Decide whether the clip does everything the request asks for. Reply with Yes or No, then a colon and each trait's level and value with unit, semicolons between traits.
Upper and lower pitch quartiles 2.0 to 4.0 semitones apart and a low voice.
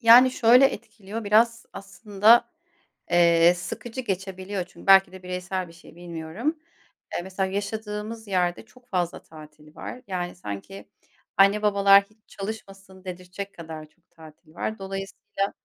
No: average, 3.3 semitones; high, 195 Hz